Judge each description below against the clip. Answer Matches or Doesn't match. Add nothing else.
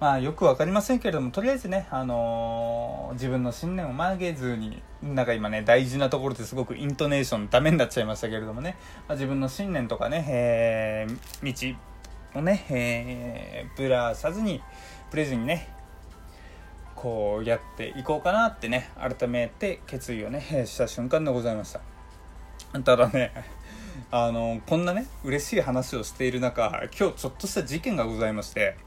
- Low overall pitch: Matches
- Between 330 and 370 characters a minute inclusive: Matches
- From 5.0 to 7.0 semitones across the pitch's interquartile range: Doesn't match